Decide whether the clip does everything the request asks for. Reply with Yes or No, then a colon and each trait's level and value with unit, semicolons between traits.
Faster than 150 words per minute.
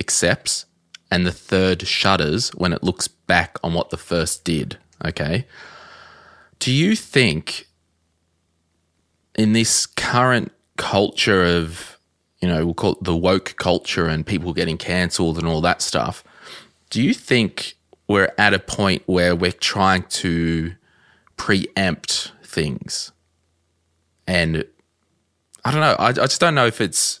No: average, 140 wpm